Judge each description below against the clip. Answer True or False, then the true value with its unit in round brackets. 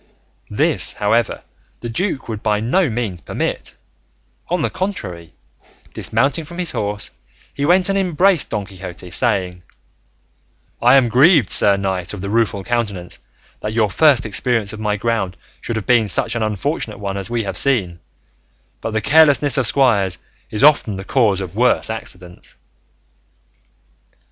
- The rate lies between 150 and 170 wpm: True (155 wpm)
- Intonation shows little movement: False (5.5 semitones)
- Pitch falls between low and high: False (110 Hz)